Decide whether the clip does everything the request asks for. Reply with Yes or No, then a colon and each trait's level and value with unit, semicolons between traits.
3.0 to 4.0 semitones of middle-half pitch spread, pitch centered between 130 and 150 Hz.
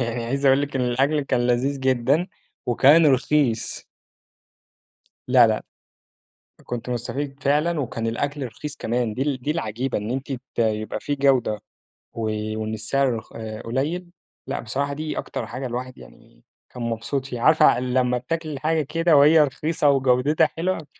Yes: average, 3.3 semitones; low, 135 Hz